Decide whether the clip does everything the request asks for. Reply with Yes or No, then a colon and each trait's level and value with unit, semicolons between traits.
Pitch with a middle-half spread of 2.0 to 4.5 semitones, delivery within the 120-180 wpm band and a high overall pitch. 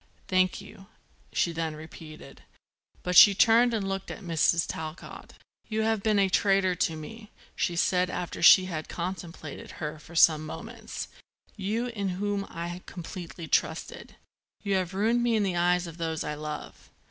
No: average, 3.4 semitones; average, 165 wpm; medium, 180 Hz